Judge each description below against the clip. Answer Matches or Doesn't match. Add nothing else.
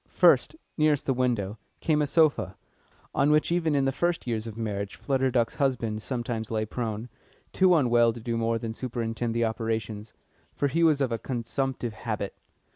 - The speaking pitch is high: Doesn't match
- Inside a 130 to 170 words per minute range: Doesn't match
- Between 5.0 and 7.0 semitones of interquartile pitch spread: Doesn't match